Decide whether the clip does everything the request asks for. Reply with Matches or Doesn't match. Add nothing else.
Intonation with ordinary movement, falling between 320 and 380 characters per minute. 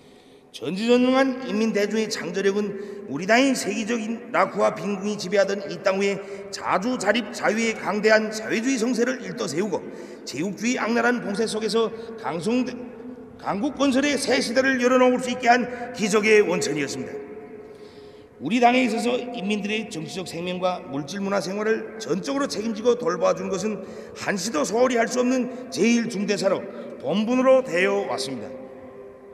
Matches